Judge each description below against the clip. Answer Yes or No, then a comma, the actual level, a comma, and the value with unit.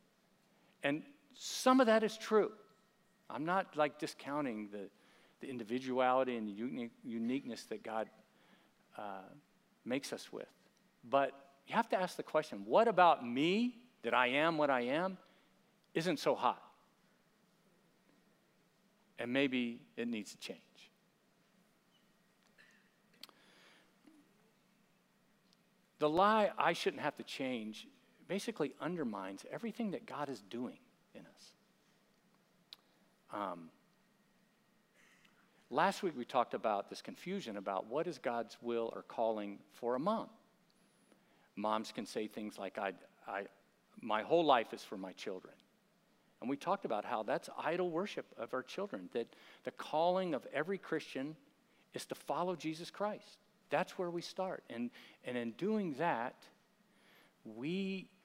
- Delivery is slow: Yes, slow, 130 wpm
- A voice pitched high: Yes, high, 195 Hz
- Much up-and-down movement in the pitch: Yes, wide, 7.4 semitones